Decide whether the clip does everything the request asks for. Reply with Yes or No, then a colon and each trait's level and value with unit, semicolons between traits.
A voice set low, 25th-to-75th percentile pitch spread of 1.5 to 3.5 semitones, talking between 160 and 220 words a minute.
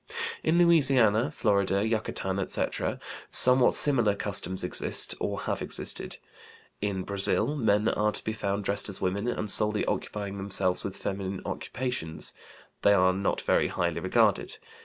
No: low, 100 Hz; narrow, 2.5 semitones; average, 140 wpm